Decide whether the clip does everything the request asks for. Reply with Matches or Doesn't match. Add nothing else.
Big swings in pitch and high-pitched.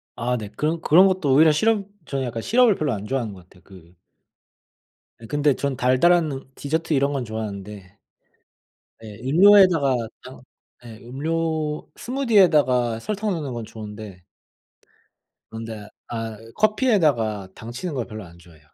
Doesn't match